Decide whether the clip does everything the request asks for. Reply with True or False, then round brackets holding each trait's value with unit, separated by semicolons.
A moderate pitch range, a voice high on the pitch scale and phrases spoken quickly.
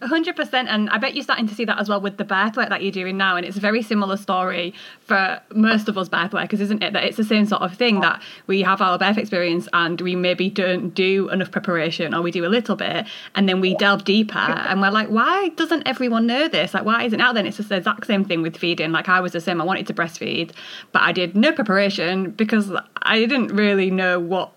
True (3.2 semitones; 195 Hz; 260 wpm)